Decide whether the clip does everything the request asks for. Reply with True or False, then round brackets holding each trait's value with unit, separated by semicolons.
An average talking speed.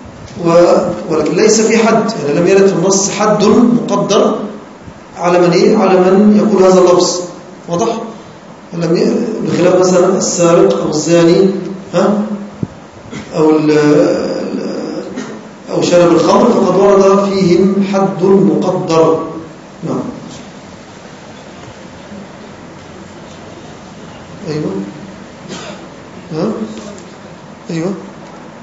False (85 wpm)